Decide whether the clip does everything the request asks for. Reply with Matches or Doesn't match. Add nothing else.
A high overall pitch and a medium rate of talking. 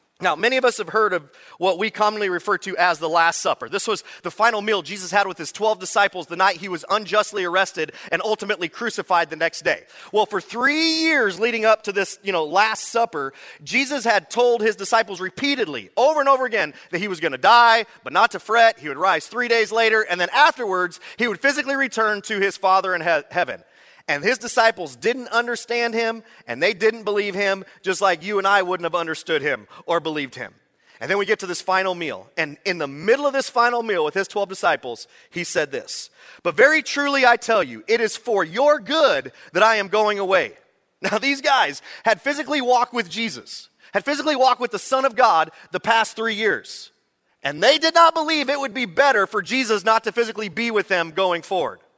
Doesn't match